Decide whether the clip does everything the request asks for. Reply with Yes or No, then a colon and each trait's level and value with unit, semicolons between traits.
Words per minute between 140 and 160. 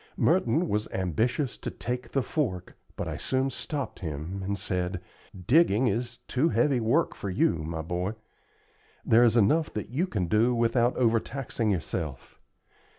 Yes: average, 155 wpm